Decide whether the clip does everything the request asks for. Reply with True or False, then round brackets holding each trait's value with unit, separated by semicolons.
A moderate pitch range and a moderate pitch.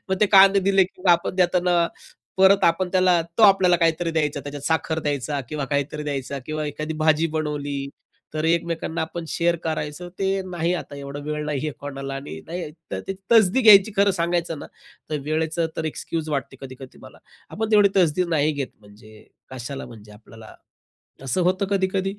True (4.2 semitones; 160 Hz)